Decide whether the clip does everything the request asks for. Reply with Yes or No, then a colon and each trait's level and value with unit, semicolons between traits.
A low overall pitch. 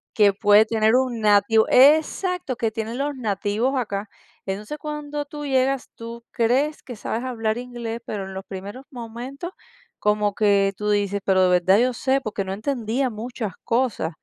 No: high, 230 Hz